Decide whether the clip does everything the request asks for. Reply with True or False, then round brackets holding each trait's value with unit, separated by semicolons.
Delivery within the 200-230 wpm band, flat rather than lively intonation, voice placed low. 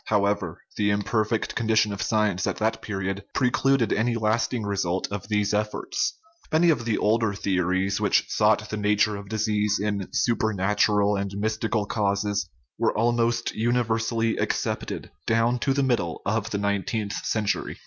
False (155 wpm; 2.1 semitones; 105 Hz)